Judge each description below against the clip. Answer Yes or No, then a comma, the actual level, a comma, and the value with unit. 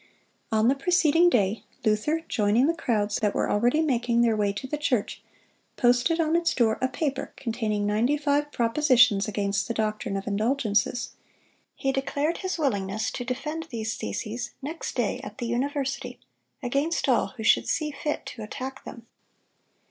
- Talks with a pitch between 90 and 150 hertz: No, high, 245 Hz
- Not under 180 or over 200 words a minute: No, average, 165 wpm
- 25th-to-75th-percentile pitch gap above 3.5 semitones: Yes, average, 5.1 semitones